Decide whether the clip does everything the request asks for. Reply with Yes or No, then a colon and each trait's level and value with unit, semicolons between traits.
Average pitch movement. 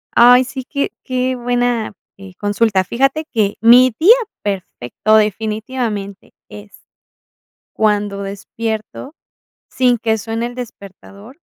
Yes: average, 3.4 semitones